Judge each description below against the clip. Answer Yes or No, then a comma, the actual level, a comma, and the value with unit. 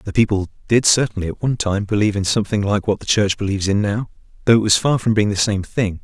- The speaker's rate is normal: No, fast, 260 wpm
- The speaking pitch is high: No, low, 105 Hz